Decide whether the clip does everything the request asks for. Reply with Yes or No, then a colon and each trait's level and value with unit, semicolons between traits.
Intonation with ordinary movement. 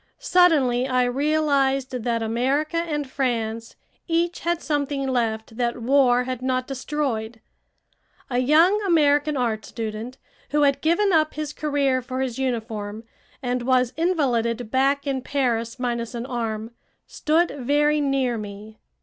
Yes: average, 3.8 semitones